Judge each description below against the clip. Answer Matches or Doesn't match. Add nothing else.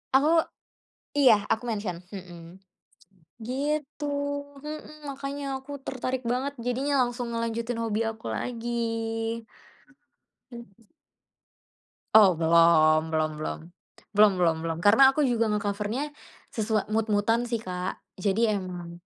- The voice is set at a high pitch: Matches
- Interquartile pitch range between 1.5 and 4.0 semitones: Doesn't match